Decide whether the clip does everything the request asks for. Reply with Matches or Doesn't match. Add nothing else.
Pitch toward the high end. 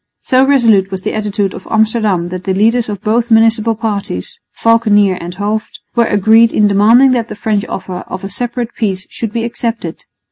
Matches